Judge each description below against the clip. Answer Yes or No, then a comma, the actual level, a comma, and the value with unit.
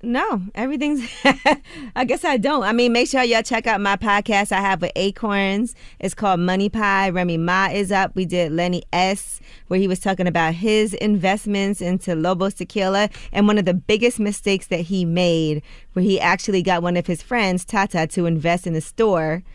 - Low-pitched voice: No, high, 195 Hz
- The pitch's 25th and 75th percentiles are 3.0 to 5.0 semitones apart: Yes, average, 3.3 semitones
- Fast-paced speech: No, average, 195 wpm